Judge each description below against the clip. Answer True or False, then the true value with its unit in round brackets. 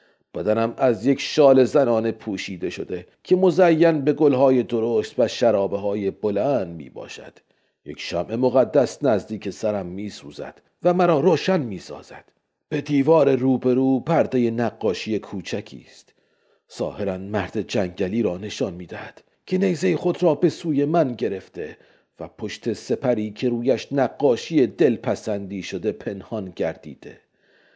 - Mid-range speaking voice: False (125 Hz)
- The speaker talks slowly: False (130 wpm)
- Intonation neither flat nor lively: False (6.1 semitones)